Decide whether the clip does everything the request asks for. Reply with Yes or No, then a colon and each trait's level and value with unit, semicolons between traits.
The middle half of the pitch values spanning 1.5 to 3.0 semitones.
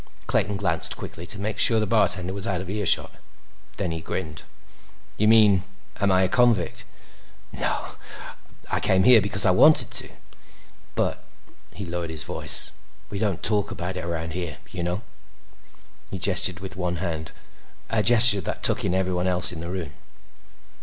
Yes: average, 2.7 semitones